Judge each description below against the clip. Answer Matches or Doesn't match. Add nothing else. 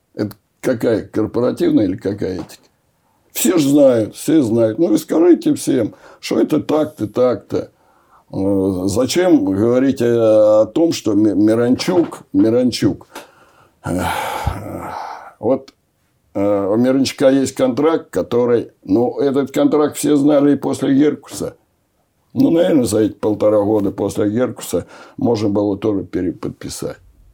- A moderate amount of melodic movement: Doesn't match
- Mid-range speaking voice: Doesn't match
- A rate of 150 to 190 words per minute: Doesn't match